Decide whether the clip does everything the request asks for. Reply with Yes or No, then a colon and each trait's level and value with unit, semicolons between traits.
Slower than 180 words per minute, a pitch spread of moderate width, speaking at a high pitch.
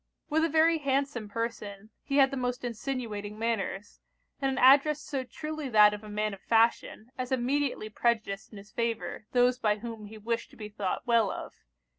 No: average, 190 wpm; average, 4.1 semitones; high, 235 Hz